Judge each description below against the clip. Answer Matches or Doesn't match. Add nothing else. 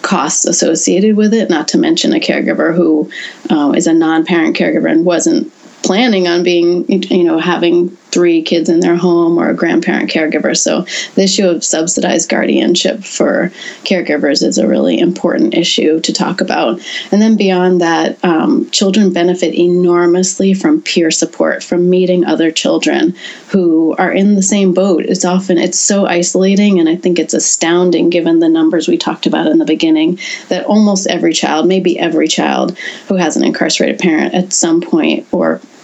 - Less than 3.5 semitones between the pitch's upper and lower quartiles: Doesn't match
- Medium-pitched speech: Matches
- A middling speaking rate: Matches